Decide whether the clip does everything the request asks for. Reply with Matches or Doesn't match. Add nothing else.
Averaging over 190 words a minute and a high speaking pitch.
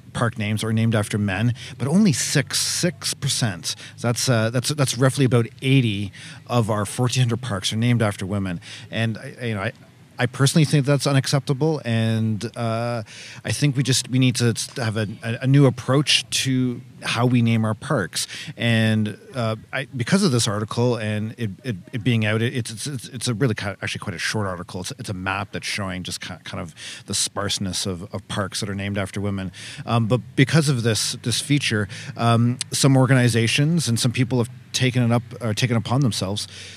Doesn't match